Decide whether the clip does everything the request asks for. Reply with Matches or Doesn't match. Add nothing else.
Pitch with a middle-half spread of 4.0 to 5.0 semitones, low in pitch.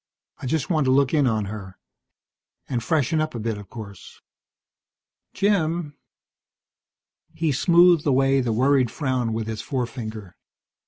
Doesn't match